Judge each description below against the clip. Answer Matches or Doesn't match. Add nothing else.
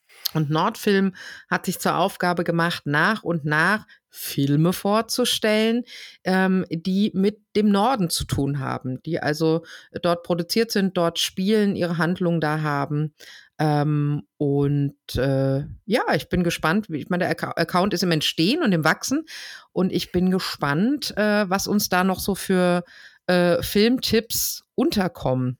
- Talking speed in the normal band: Matches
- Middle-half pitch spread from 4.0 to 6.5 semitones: Matches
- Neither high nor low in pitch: Matches